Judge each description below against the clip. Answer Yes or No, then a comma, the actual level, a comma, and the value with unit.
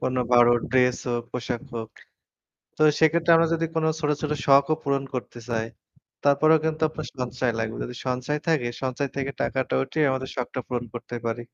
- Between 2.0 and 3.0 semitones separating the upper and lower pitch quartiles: No, average, 3.8 semitones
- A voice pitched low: Yes, low, 130 Hz